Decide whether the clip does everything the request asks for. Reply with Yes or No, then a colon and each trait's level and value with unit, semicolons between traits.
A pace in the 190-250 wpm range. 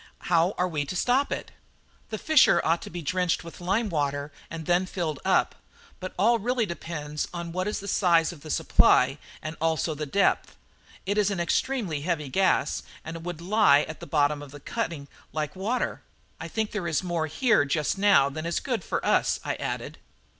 Yes: average, 195 wpm